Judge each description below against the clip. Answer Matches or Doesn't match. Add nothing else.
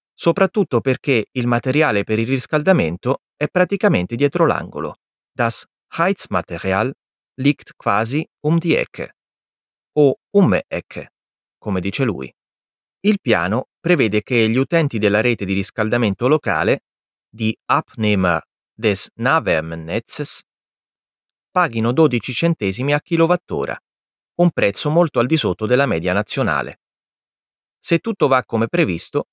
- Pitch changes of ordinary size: Doesn't match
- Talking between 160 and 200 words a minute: Doesn't match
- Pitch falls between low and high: Doesn't match